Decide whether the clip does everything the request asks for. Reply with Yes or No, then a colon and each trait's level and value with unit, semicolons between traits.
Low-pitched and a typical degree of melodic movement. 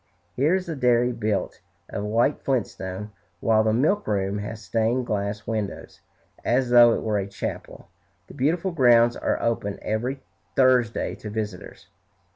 Yes: low, 115 Hz; average, 3.4 semitones